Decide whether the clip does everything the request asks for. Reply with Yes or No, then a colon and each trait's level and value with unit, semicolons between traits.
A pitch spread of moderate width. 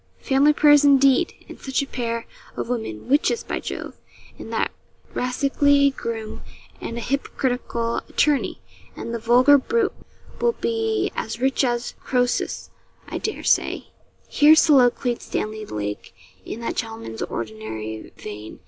Yes: average, 4.0 semitones